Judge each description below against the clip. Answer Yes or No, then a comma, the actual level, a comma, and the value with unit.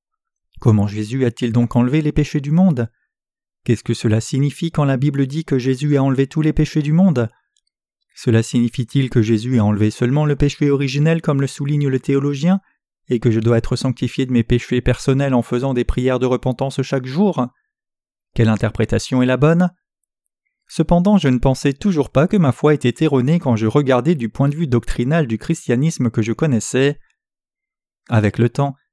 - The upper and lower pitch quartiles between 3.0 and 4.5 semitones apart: Yes, average, 3.9 semitones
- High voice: No, low, 135 Hz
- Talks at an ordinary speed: Yes, average, 190 wpm